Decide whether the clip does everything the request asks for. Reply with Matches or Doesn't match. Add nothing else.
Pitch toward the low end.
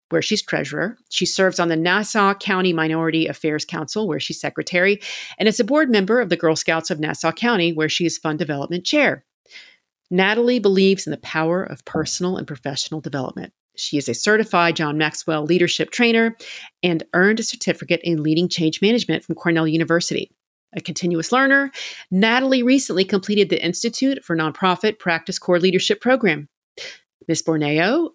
Doesn't match